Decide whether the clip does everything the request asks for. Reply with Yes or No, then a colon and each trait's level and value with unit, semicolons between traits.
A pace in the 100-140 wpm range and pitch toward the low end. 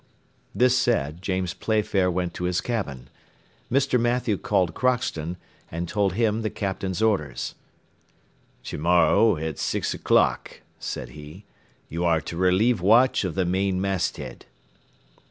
Yes: slow, 135 wpm; very low, 95 Hz